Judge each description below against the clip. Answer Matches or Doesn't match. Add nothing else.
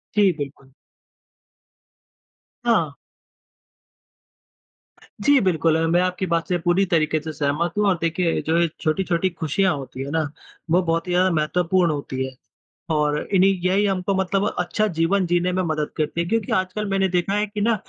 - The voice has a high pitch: Doesn't match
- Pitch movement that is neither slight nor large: Matches